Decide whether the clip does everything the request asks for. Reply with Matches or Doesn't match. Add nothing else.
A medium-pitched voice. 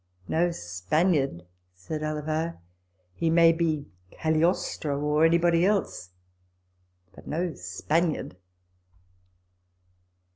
Matches